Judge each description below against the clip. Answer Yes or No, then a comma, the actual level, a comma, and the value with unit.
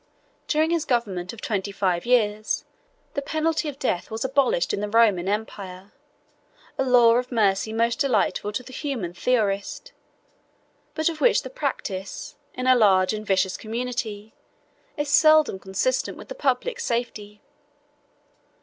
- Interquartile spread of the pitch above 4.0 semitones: Yes, average, 5.2 semitones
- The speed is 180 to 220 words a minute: No, average, 145 wpm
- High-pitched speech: Yes, high, 230 Hz